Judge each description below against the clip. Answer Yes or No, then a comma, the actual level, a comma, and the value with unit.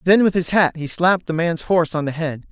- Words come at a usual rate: No, fast, 285 wpm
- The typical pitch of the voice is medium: Yes, medium, 170 Hz